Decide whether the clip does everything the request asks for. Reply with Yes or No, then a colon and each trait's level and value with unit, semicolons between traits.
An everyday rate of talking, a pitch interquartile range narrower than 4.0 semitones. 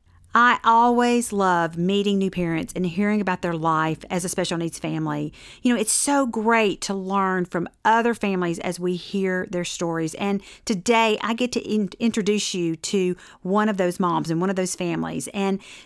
Yes: average, 190 wpm; average, 3.5 semitones